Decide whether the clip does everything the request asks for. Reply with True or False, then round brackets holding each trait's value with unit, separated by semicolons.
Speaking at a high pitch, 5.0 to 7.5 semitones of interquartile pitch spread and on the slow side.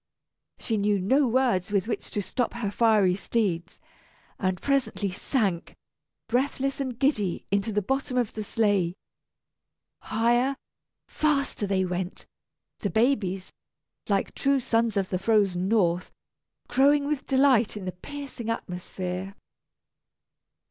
True (215 Hz; 5.4 semitones; 125 wpm)